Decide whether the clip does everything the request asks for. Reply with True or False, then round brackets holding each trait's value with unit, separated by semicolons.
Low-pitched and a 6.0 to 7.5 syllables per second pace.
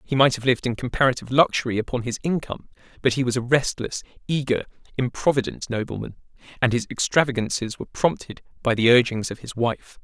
True (125 Hz; 6.4 syllables/s)